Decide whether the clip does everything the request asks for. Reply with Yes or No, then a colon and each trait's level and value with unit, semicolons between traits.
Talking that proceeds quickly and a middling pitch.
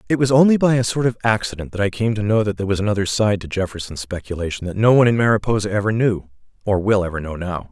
No: fast, 255 wpm; low, 105 Hz